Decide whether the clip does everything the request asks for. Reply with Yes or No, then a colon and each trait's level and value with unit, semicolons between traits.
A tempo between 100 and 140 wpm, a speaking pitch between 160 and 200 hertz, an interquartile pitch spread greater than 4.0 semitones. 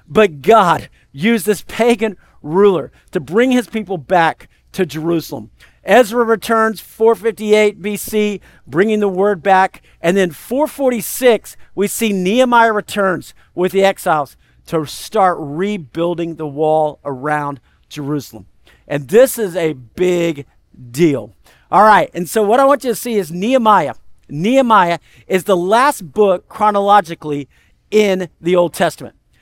Yes: slow, 135 wpm; high, 190 Hz; wide, 5.5 semitones